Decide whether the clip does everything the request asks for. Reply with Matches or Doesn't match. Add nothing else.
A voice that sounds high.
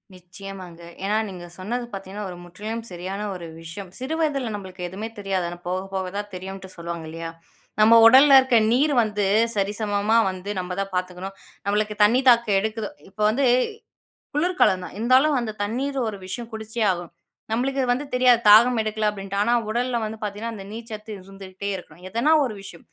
Matches